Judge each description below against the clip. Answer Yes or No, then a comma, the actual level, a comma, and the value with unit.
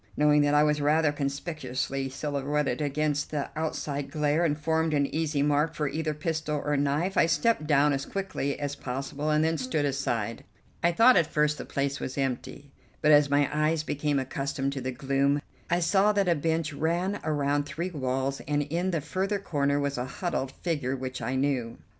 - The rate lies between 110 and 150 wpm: No, average, 190 wpm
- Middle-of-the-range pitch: Yes, medium, 145 Hz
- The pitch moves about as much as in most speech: No, narrow, 2.3 semitones